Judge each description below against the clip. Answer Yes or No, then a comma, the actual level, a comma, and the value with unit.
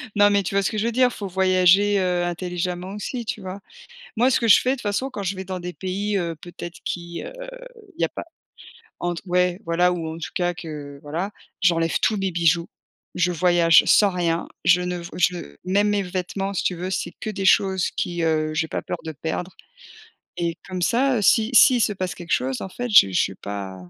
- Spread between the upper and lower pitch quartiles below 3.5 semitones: Yes, average, 2.8 semitones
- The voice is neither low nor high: Yes, medium, 180 Hz